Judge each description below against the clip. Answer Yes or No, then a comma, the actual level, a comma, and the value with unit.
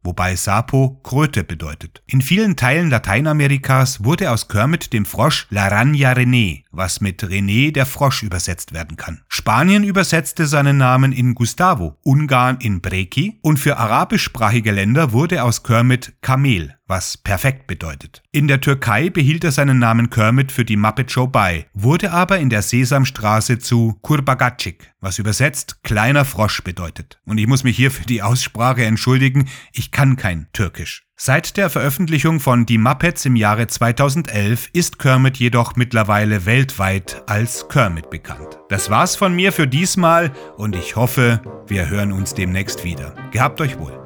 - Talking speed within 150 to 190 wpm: Yes, average, 155 wpm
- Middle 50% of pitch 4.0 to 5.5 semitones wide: Yes, average, 5.2 semitones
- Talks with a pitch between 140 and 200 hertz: No, low, 125 Hz